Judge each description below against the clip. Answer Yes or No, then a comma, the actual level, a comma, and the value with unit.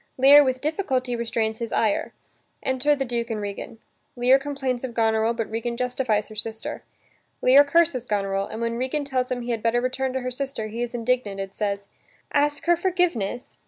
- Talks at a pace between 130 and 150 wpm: No, average, 190 wpm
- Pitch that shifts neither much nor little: Yes, average, 3.1 semitones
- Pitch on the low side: No, high, 245 Hz